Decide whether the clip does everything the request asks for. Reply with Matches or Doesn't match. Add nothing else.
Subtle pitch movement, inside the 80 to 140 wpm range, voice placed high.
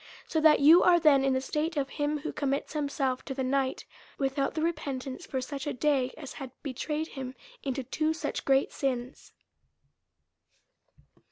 Doesn't match